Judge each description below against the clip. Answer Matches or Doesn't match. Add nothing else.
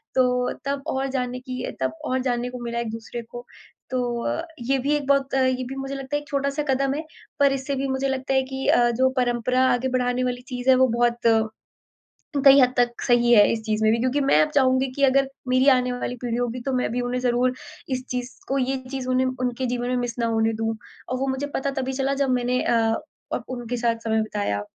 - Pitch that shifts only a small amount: Matches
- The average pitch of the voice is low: Doesn't match